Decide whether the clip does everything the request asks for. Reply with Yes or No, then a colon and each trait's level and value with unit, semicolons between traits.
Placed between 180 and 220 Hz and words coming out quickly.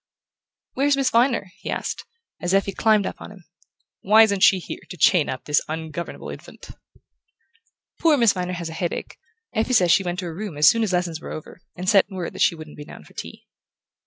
Yes: medium, 185 Hz; fast, 215 wpm